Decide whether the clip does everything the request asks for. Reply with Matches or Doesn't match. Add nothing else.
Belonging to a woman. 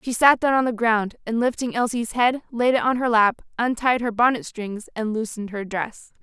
Matches